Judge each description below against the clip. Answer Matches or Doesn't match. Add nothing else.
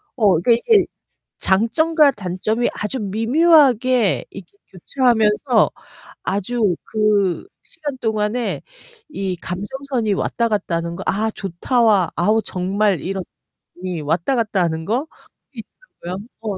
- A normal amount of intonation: Matches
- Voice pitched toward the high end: Matches